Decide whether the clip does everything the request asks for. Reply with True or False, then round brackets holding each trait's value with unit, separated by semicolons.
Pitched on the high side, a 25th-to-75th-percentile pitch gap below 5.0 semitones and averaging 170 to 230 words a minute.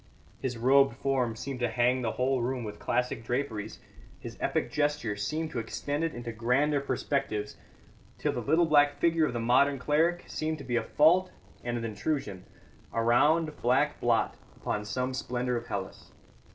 False (125 Hz; 3.8 semitones; 175 wpm)